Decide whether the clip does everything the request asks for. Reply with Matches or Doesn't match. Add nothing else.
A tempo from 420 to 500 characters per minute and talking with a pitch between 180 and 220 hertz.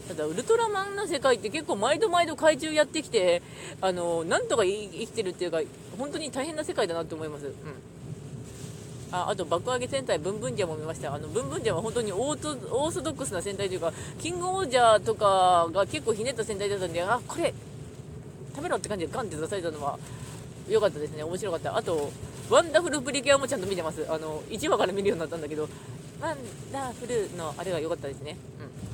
Matches